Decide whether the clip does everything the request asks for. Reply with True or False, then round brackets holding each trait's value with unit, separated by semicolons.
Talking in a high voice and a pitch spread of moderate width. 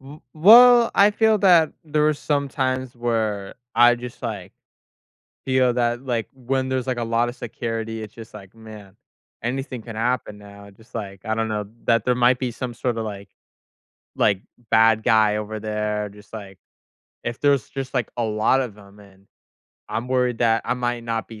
False (115 Hz; 3.1 semitones)